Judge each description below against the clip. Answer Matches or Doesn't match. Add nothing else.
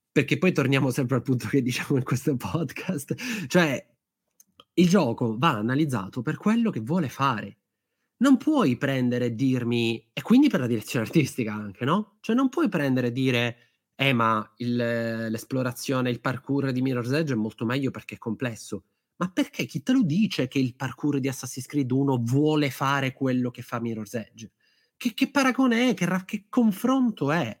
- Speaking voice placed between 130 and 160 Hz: Matches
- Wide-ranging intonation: Matches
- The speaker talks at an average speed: Doesn't match